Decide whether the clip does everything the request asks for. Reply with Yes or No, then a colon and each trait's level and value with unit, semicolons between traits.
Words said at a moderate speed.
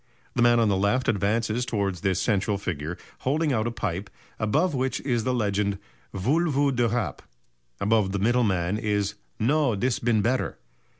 Yes: average, 175 wpm